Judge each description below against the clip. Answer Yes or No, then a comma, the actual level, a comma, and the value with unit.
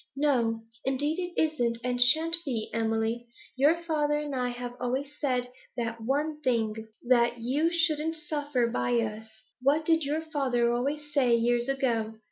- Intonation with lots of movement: No, average, 4.0 semitones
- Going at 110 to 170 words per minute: Yes, average, 155 wpm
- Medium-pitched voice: No, very high, 255 Hz